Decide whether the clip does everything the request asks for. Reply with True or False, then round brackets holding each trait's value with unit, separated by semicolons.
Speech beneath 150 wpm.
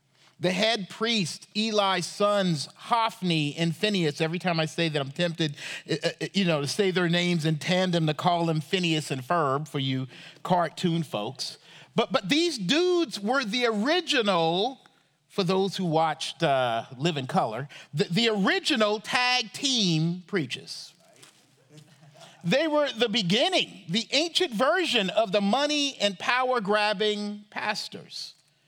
True (140 wpm)